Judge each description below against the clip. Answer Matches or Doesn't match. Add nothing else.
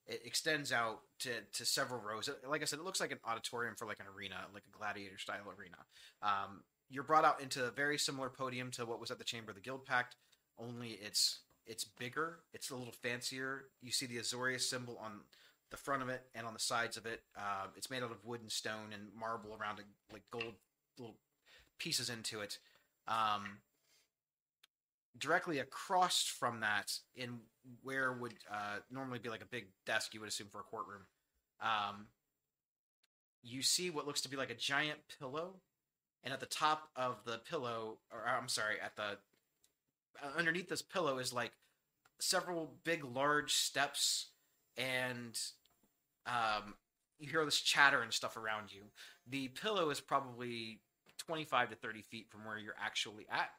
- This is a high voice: Doesn't match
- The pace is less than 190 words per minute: Matches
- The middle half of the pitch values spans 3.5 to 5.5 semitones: Matches